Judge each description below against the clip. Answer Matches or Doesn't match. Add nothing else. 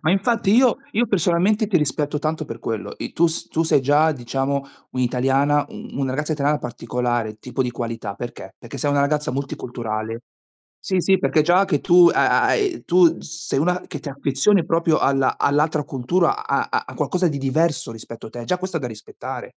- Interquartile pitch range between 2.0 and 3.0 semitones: Doesn't match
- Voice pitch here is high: Doesn't match